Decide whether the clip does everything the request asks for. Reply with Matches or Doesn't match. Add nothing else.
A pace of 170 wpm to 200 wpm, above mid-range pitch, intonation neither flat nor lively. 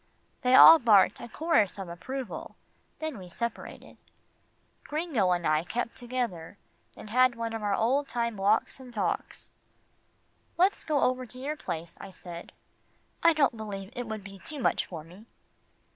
Doesn't match